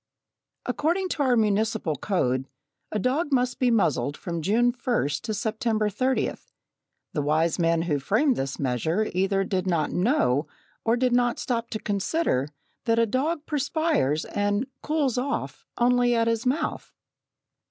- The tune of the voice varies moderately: No, wide, 6.6 semitones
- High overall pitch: Yes, high, 225 Hz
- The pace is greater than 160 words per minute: No, average, 150 wpm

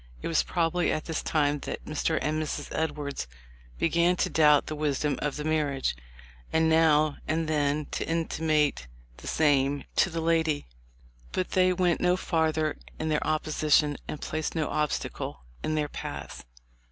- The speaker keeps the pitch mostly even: Yes, narrow, 1.5 semitones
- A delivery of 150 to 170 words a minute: Yes, average, 165 wpm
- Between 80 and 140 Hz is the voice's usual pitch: No, medium, 155 Hz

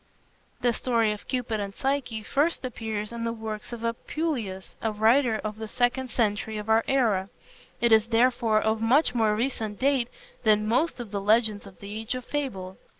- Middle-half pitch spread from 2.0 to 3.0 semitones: Yes, average, 2.7 semitones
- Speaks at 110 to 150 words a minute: No, average, 185 wpm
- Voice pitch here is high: Yes, high, 225 Hz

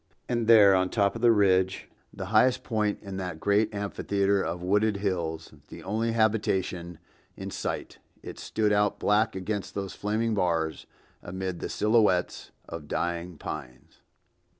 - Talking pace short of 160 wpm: Yes, average, 150 wpm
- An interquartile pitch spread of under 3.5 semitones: Yes, average, 3.0 semitones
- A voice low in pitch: Yes, low, 100 Hz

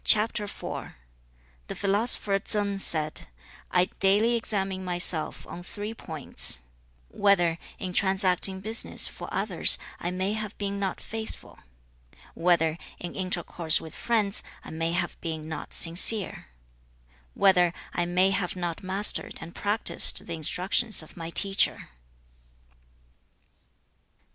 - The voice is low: No, medium, 185 Hz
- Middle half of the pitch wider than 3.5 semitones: No, average, 3.2 semitones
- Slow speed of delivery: Yes, slow, 115 wpm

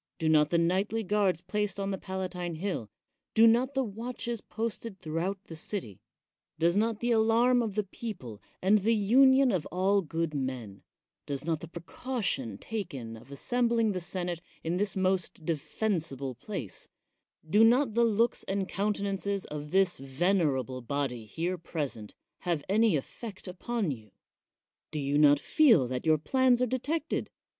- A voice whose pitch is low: No, medium, 185 Hz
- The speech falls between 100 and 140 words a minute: No, average, 165 wpm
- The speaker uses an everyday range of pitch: No, wide, 6.3 semitones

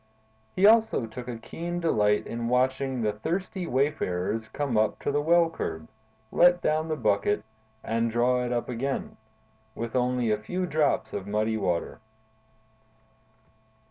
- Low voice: Yes, low, 125 Hz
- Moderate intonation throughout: No, wide, 6.1 semitones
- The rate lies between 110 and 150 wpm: Yes, average, 145 wpm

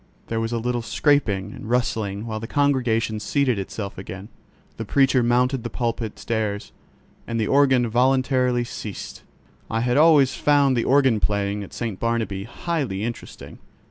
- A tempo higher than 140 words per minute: Yes, average, 155 wpm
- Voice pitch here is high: No, low, 115 Hz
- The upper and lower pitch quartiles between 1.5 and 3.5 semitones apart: Yes, average, 3.2 semitones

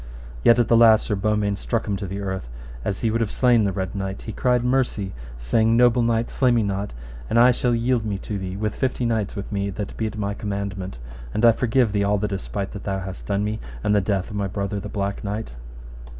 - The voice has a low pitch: Yes, low, 105 Hz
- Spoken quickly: Yes, fast, 250 wpm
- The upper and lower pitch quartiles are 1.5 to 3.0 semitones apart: Yes, narrow, 2.6 semitones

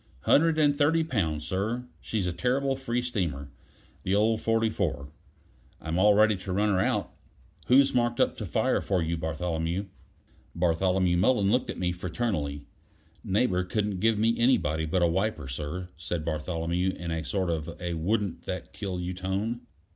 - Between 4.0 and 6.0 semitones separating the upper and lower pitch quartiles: Yes, average, 4.9 semitones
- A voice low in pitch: Yes, very low, 95 Hz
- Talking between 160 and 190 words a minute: Yes, average, 165 wpm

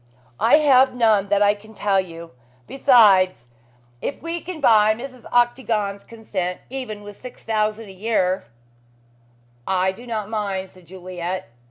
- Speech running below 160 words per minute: Yes, average, 150 wpm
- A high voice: Yes, high, 205 Hz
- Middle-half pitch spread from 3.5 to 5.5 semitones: Yes, average, 4.0 semitones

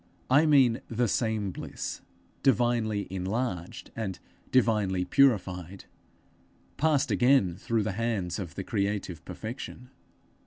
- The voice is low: Yes, low, 110 Hz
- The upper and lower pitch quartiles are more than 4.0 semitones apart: Yes, average, 4.5 semitones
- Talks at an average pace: No, slow, 115 wpm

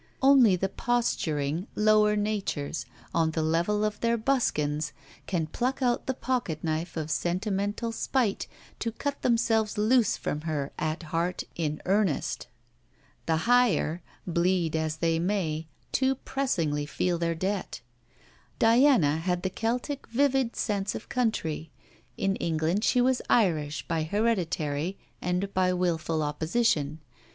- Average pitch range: No, wide, 6.2 semitones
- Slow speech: Yes, slow, 130 wpm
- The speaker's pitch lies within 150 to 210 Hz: Yes, medium, 185 Hz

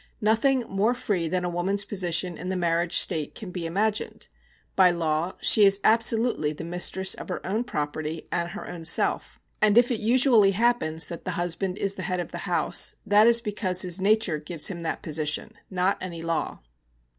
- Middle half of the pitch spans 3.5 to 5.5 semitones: Yes, average, 3.9 semitones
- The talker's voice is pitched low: No, medium, 185 Hz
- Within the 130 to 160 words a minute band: No, average, 190 wpm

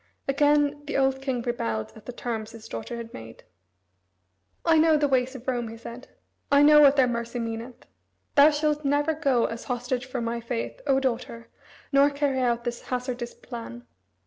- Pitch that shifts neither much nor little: Yes, average, 3.3 semitones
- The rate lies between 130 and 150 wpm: No, average, 180 wpm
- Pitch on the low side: No, very high, 250 Hz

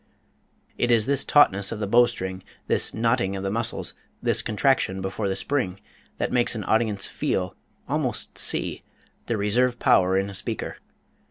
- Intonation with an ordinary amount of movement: Yes, average, 3.7 semitones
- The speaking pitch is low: Yes, low, 105 Hz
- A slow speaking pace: No, average, 165 wpm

